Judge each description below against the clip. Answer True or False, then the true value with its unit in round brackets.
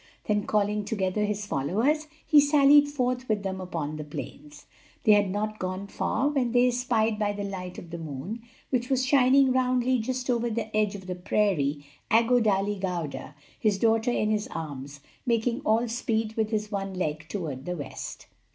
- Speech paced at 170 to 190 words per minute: True (180 wpm)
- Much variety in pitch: False (4.8 semitones)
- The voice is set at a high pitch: True (215 Hz)